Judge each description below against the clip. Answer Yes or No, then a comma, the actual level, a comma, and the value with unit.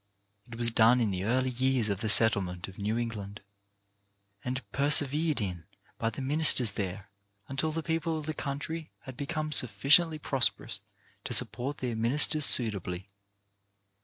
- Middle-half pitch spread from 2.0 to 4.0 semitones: No, wide, 5.6 semitones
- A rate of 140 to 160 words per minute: Yes, average, 150 wpm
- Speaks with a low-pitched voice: Yes, low, 125 Hz